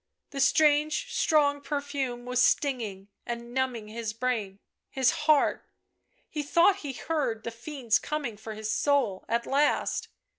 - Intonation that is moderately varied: Yes, average, 4.2 semitones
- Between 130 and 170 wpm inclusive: Yes, average, 145 wpm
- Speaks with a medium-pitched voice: No, very high, 260 Hz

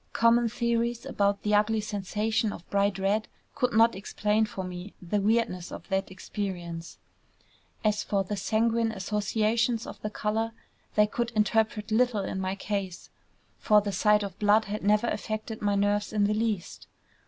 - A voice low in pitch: No, high, 210 Hz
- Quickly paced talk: No, average, 165 wpm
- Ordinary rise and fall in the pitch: No, narrow, 1.8 semitones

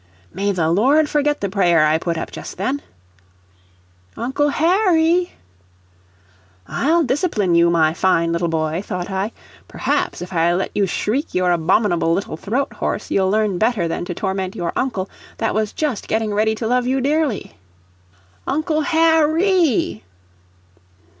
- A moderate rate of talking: Yes, average, 150 wpm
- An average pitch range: No, wide, 8.7 semitones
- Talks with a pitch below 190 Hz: No, high, 210 Hz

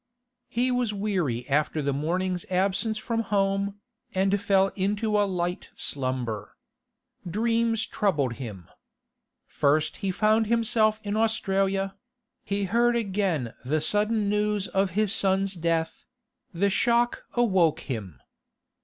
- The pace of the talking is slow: Yes, slow, 120 wpm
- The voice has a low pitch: No, high, 195 Hz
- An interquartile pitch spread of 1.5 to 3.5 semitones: No, average, 4.5 semitones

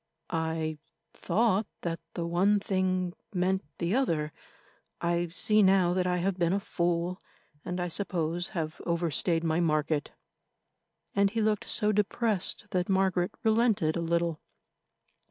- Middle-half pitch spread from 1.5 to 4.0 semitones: Yes, average, 2.7 semitones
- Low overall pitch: No, medium, 180 Hz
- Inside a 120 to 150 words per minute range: Yes, slow, 135 wpm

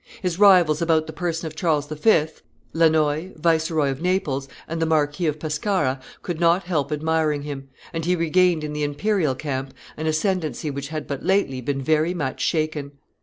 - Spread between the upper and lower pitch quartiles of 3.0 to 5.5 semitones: No, narrow, 2.4 semitones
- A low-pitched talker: No, medium, 155 Hz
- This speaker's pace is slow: No, average, 175 wpm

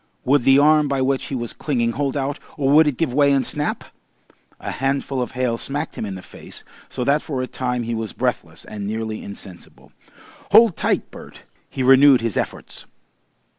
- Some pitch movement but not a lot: Yes, average, 3.4 semitones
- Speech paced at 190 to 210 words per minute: Yes, average, 195 wpm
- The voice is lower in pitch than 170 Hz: Yes, low, 135 Hz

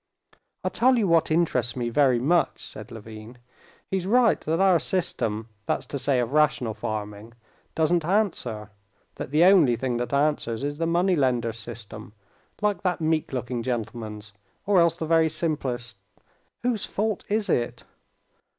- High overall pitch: No, medium, 140 Hz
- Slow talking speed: No, average, 155 wpm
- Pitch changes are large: Yes, wide, 6.7 semitones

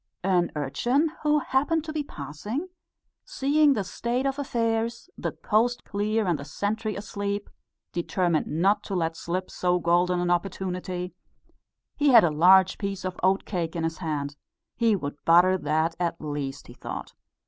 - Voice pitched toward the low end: No, high, 190 Hz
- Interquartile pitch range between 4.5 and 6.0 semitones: Yes, wide, 5.4 semitones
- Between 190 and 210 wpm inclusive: No, average, 160 wpm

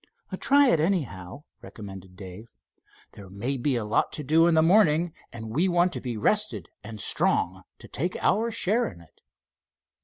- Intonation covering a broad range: Yes, wide, 9.0 semitones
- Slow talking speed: No, average, 175 wpm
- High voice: No, medium, 140 Hz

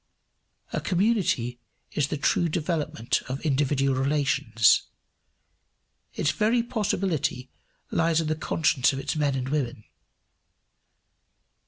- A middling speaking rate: No, slow, 110 wpm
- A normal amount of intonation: Yes, average, 4.0 semitones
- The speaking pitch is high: No, medium, 150 Hz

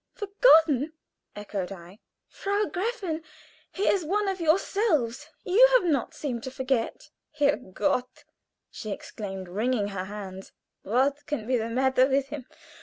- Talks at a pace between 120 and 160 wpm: Yes, slow, 135 wpm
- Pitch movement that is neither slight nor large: No, wide, 8.2 semitones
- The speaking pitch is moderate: No, very high, 265 Hz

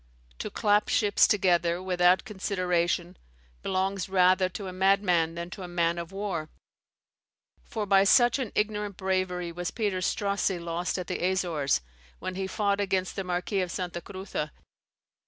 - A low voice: No, medium, 185 Hz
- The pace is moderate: Yes, average, 155 wpm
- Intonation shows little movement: Yes, narrow, 2.1 semitones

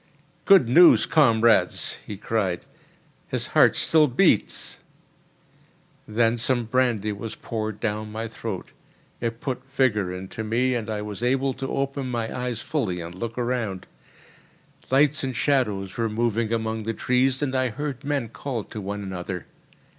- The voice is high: No, low, 115 Hz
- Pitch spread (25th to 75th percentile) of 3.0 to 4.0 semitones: Yes, average, 3.5 semitones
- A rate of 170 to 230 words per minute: No, average, 150 wpm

